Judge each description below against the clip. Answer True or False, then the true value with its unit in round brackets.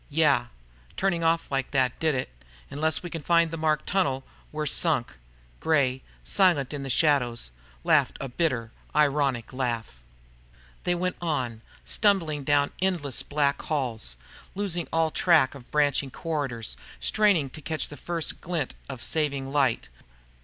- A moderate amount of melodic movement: True (3.8 semitones)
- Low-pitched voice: False (145 Hz)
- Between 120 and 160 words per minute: True (145 wpm)